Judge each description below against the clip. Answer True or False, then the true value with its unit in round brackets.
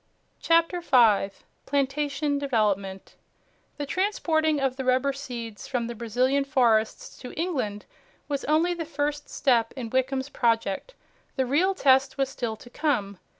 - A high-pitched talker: True (270 Hz)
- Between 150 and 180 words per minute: False (140 wpm)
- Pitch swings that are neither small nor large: True (4.0 semitones)